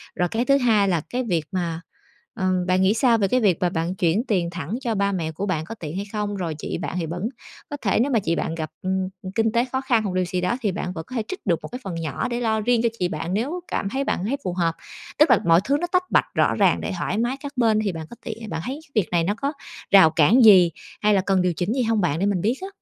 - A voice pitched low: No, high, 200 Hz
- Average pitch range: Yes, average, 5.0 semitones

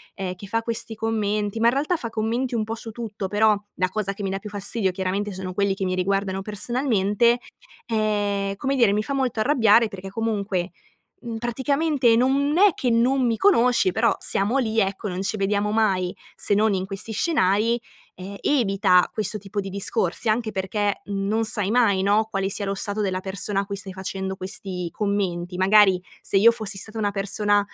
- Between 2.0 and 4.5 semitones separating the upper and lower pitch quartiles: Yes, average, 2.7 semitones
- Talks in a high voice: Yes, high, 205 Hz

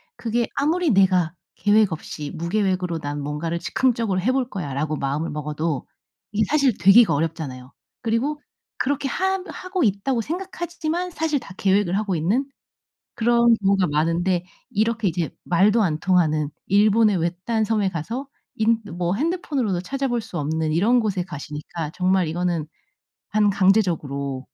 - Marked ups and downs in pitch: Yes, wide, 6.2 semitones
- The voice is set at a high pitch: Yes, high, 195 Hz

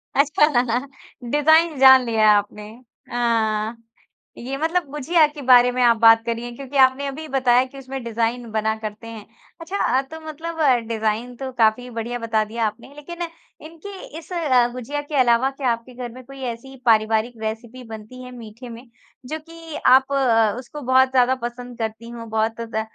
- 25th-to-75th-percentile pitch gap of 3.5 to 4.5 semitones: No, average, 3.1 semitones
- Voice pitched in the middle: No, high, 245 Hz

